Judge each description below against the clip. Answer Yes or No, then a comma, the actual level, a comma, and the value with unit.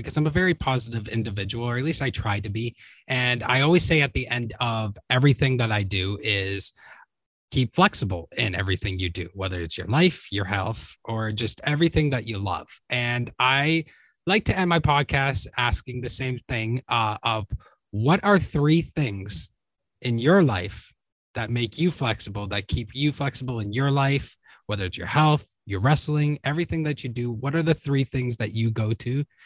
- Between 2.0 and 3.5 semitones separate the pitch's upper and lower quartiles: No, average, 5.2 semitones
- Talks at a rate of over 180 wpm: Yes, average, 190 wpm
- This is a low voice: Yes, low, 120 Hz